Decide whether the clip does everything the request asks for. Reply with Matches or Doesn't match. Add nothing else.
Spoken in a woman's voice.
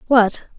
Matches